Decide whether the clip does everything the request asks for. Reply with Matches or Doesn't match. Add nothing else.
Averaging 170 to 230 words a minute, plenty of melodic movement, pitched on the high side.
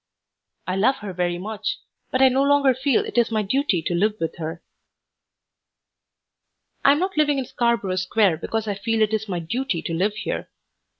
Matches